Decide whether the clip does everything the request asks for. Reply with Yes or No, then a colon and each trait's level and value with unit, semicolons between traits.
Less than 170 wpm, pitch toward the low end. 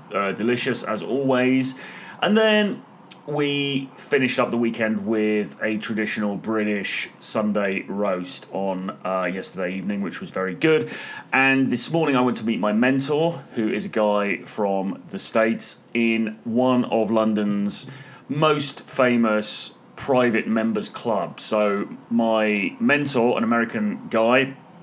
Yes: slow, 135 wpm; low, 115 Hz